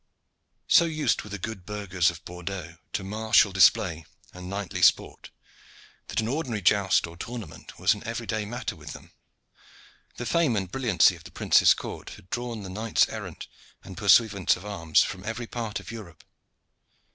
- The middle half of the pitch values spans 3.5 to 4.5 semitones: Yes, average, 3.8 semitones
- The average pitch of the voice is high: No, low, 105 Hz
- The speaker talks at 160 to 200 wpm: Yes, average, 170 wpm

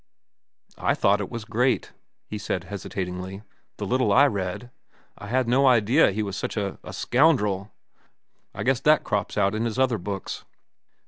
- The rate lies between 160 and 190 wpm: Yes, average, 165 wpm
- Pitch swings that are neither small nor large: Yes, average, 4.2 semitones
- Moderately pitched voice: No, low, 110 Hz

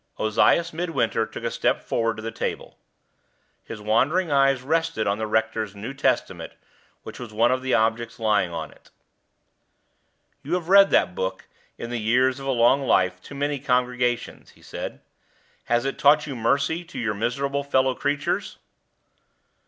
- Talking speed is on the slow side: No, average, 165 wpm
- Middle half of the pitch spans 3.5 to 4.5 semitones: Yes, average, 4.2 semitones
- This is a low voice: Yes, low, 125 Hz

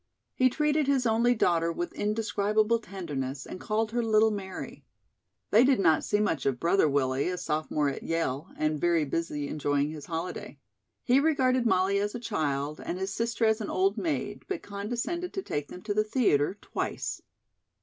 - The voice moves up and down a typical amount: No, wide, 6.7 semitones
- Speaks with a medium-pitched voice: No, high, 200 Hz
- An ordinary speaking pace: Yes, average, 180 wpm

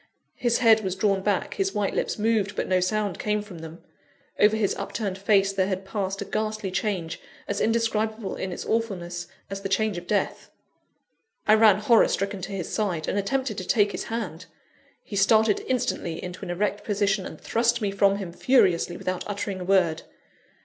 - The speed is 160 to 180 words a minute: No, average, 190 wpm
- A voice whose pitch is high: Yes, high, 200 Hz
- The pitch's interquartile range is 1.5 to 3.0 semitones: Yes, narrow, 2.4 semitones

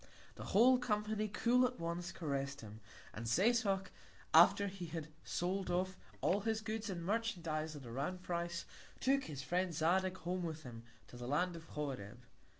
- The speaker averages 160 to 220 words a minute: Yes, average, 170 wpm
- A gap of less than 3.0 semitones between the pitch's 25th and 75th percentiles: No, average, 4.7 semitones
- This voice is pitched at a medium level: Yes, medium, 175 Hz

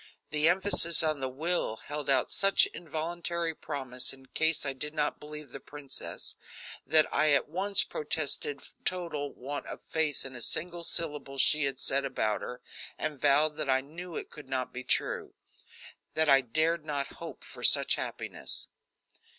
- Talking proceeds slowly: No, average, 165 wpm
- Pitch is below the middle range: No, medium, 150 Hz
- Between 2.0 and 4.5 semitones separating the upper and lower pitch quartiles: Yes, average, 2.8 semitones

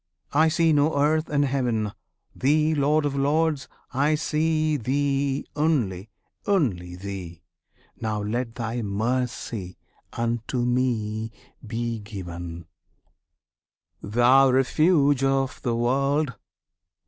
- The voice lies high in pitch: No, low, 130 Hz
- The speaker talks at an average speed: No, slow, 100 wpm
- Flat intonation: No, average, 4.7 semitones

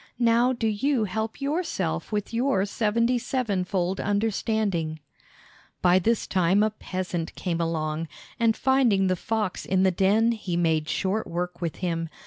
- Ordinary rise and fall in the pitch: Yes, average, 4.5 semitones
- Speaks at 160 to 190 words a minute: No, average, 145 wpm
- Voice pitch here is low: No, high, 200 Hz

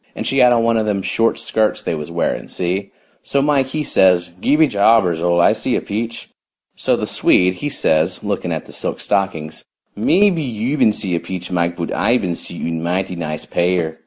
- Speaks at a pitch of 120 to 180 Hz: No, very low, 95 Hz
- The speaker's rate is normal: No, fast, 215 wpm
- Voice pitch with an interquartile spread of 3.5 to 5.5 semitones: Yes, average, 5.1 semitones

